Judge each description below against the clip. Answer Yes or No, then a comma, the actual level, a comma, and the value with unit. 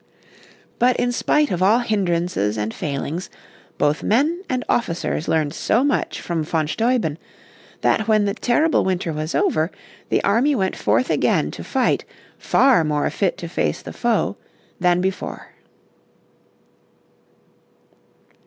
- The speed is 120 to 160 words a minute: Yes, slow, 135 wpm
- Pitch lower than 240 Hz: Yes, high, 190 Hz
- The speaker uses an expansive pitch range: Yes, wide, 6.9 semitones